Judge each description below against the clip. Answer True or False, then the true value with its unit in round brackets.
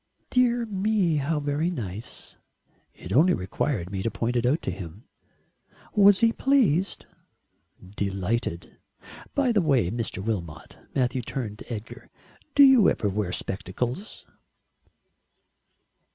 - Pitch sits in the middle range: False (125 Hz)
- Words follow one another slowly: True (125 wpm)